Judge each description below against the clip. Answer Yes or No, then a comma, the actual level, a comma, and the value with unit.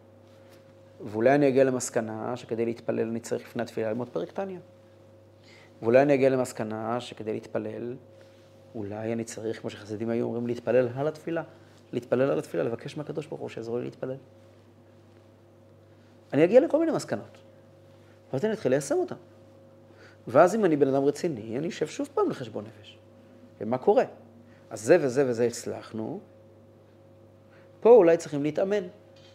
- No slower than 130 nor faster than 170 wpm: Yes, average, 145 wpm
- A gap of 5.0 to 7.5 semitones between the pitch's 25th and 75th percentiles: No, narrow, 2.6 semitones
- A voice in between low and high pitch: No, low, 110 Hz